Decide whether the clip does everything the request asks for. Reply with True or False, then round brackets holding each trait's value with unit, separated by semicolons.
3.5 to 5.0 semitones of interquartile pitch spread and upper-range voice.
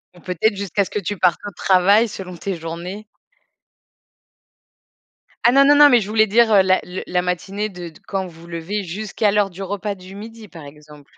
False (2.9 semitones; 195 Hz)